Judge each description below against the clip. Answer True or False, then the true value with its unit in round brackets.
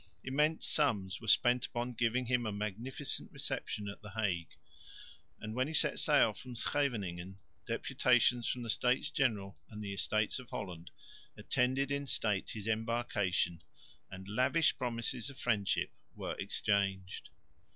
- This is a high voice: False (115 Hz)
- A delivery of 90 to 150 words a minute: True (140 wpm)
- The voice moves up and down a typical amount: True (4.0 semitones)